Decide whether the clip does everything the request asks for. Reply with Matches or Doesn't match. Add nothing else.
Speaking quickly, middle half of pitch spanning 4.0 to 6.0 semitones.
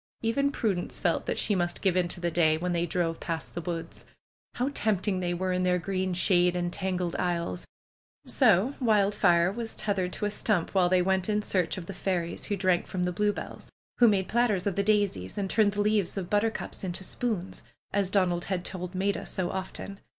Doesn't match